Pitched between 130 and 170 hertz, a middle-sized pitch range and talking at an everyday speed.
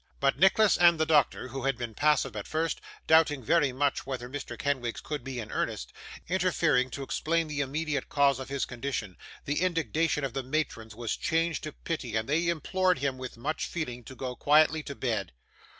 Yes: medium, 140 Hz; average, 3.8 semitones; average, 195 wpm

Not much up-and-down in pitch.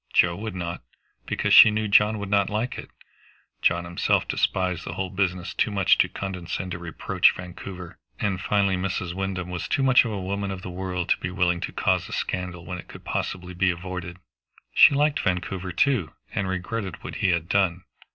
Yes: narrow, 2.0 semitones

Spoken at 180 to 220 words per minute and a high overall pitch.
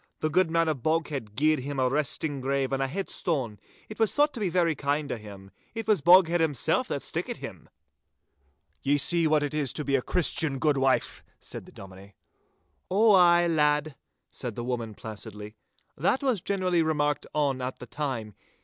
No: average, 185 wpm; medium, 150 Hz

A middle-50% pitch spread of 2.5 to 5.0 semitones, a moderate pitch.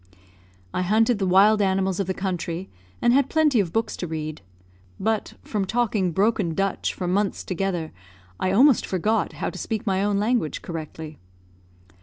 No: average, 3.5 semitones; high, 195 Hz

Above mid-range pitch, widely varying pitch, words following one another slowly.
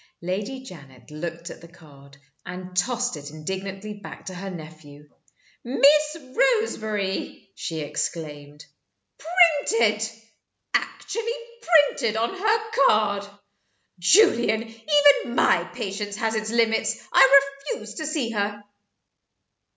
Yes: high, 210 Hz; wide, 6.9 semitones; slow, 110 wpm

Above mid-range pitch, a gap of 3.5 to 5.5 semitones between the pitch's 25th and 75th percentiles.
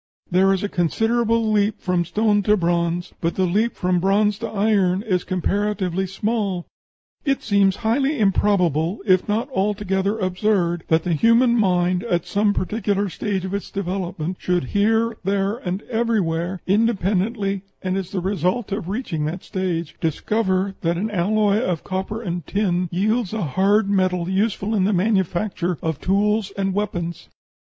No: high, 195 Hz; average, 2.8 semitones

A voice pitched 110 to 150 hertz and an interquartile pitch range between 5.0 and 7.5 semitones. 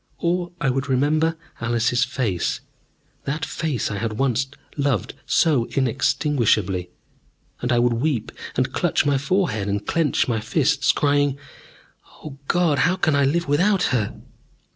No: low, 135 Hz; average, 4.6 semitones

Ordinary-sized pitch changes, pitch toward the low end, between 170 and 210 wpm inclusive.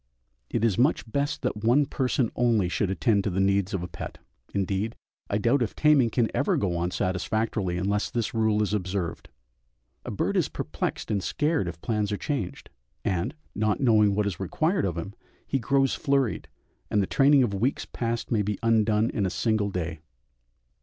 Yes: average, 3.8 semitones; low, 105 Hz; average, 185 wpm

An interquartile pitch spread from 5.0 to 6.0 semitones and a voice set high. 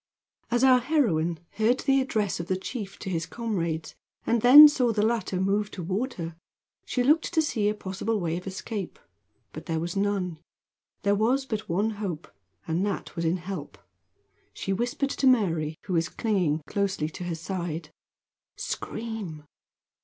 Yes: average, 5.3 semitones; high, 200 Hz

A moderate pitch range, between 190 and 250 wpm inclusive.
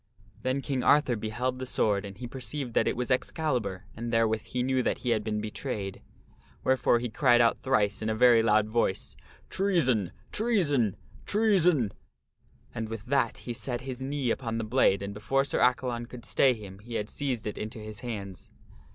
Yes: average, 3.4 semitones; average, 195 wpm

